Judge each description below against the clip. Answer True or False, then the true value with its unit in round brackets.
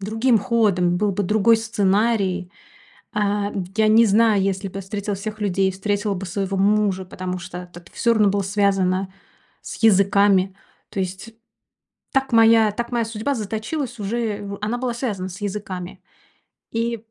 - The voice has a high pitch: True (205 Hz)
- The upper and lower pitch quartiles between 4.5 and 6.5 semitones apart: False (2.7 semitones)